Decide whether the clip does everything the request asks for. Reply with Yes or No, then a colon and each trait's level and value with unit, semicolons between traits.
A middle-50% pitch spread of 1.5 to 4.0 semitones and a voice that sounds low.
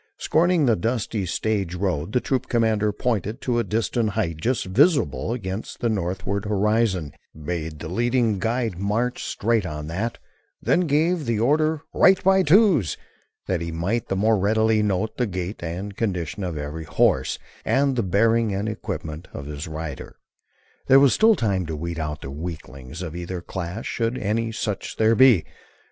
No: average, 5.3 semitones; low, 105 Hz